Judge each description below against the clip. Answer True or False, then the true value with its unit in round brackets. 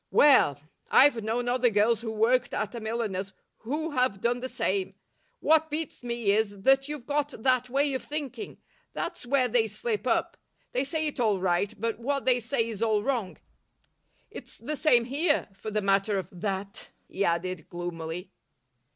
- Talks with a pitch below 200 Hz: False (235 Hz)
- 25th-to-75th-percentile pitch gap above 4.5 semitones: True (5.2 semitones)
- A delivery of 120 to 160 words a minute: False (175 wpm)